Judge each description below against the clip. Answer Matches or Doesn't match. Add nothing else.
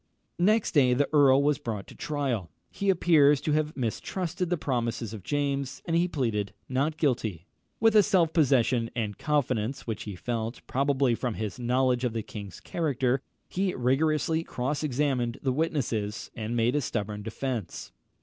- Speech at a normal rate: Matches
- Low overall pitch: Matches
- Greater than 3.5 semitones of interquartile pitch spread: Matches